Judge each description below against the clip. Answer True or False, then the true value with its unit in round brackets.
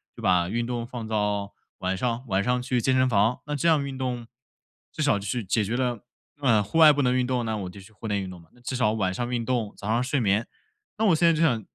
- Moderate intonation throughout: True (3.8 semitones)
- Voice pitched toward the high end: False (120 Hz)